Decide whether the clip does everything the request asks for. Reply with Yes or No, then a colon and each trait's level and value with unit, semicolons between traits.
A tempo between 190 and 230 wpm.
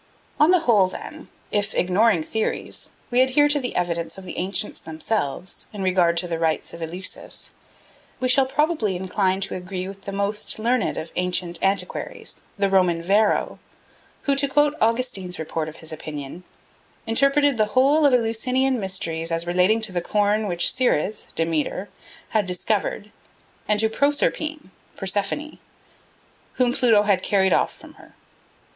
No: average, 155 wpm